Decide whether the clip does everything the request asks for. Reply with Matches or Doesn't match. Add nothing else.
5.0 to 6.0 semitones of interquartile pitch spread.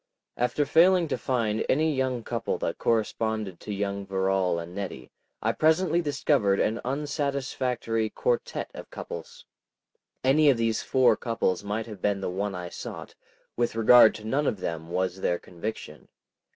Matches